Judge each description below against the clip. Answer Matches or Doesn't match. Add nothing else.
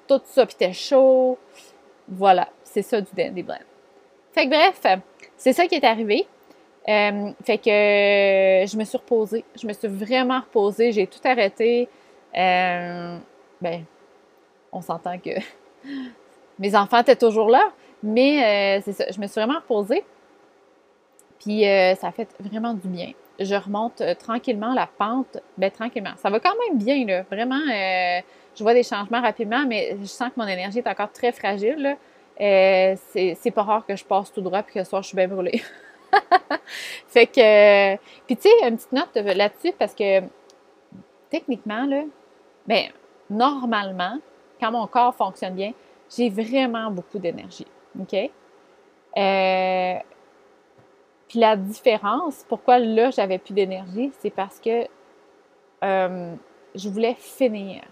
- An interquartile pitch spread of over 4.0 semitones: Matches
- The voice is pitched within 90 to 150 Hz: Doesn't match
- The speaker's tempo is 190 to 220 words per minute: Doesn't match